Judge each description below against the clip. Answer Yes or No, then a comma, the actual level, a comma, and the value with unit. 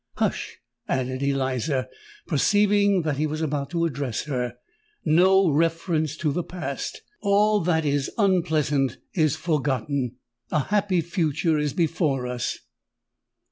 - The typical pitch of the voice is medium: Yes, medium, 155 Hz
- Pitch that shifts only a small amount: No, average, 4.2 semitones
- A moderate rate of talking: No, slow, 120 wpm